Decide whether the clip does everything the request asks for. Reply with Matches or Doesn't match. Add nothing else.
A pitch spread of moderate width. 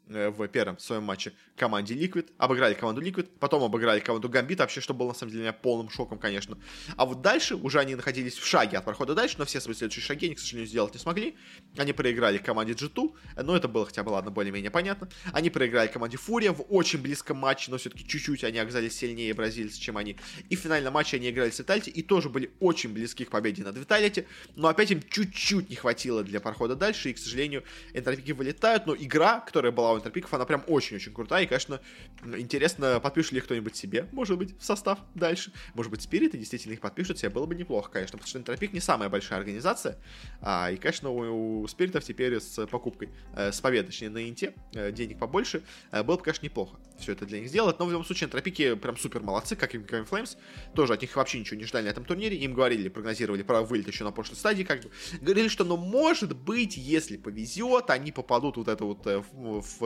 Doesn't match